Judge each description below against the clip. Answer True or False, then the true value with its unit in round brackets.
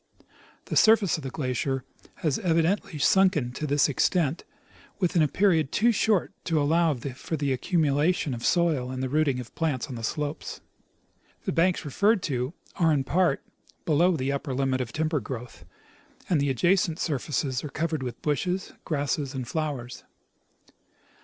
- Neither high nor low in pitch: True (150 Hz)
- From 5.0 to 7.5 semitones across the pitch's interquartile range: False (4.2 semitones)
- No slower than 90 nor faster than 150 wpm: False (160 wpm)